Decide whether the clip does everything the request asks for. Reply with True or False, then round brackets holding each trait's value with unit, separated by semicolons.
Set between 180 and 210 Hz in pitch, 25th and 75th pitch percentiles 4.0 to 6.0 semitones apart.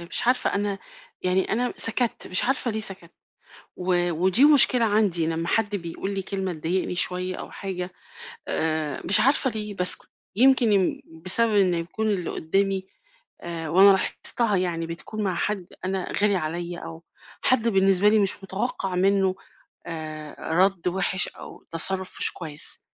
False (190 Hz; 3.1 semitones)